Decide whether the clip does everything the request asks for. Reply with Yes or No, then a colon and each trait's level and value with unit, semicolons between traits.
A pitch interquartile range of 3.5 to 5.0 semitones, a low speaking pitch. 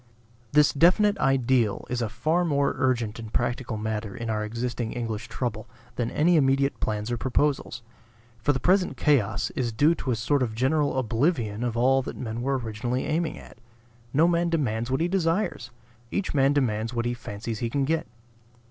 Yes: average, 4.4 semitones; low, 125 Hz